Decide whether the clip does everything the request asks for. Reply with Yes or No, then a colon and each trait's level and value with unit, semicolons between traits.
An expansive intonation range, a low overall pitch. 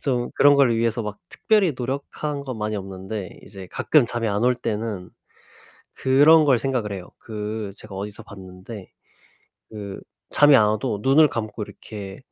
No: average, 4.5 semitones; low, 110 Hz